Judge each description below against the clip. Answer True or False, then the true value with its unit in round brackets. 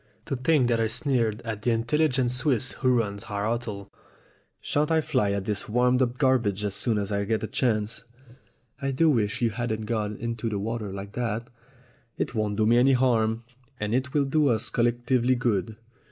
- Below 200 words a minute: False (205 wpm)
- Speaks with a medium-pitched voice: False (115 Hz)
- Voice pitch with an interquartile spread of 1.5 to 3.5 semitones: True (3.0 semitones)